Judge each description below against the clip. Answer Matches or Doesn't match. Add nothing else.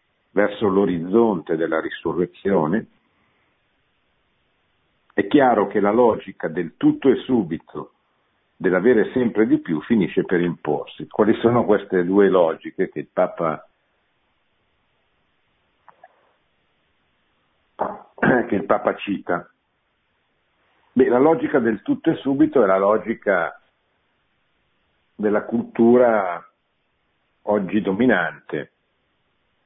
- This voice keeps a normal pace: Doesn't match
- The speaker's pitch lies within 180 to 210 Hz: Doesn't match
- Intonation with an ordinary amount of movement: Matches